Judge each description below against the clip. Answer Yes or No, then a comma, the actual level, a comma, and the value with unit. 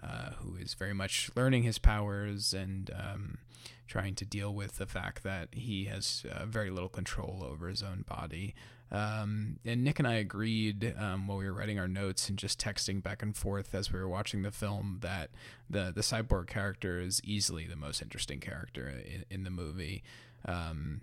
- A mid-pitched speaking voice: No, low, 100 Hz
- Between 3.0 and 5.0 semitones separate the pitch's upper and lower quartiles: No, narrow, 2.4 semitones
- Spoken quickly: No, average, 195 wpm